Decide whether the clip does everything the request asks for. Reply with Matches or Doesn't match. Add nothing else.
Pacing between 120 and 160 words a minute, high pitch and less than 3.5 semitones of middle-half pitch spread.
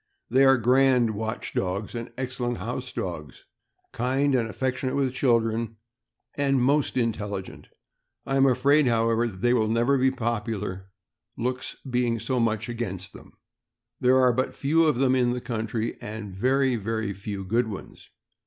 Doesn't match